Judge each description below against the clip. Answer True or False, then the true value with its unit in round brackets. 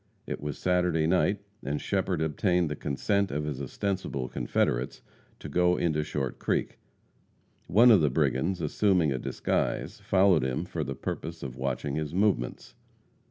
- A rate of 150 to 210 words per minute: True (155 wpm)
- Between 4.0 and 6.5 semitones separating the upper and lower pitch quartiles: True (4.8 semitones)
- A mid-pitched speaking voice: False (80 Hz)